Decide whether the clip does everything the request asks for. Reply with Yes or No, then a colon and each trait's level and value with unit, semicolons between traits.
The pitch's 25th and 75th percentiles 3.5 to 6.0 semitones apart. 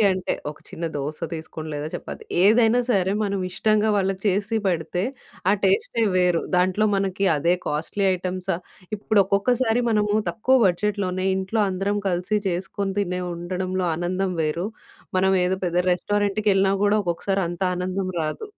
No: narrow, 2.4 semitones